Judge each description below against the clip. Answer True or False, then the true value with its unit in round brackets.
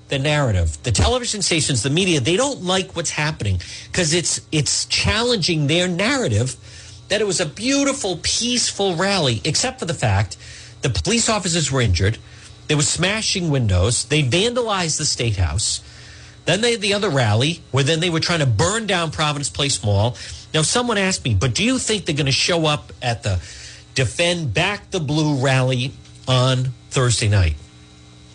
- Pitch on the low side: False (150 Hz)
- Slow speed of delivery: False (175 wpm)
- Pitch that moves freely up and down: True (8.1 semitones)